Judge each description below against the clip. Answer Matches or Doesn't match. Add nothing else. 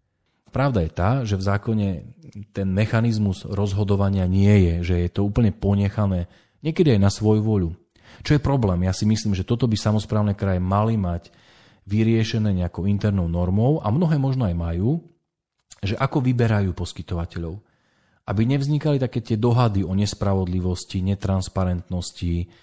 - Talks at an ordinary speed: Matches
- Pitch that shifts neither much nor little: Matches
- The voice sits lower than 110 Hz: Matches